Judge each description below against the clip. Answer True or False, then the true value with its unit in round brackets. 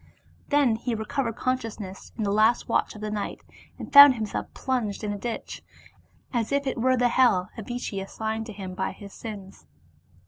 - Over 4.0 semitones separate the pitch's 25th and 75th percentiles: False (3.3 semitones)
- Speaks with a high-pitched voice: True (220 Hz)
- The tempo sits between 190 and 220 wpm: False (180 wpm)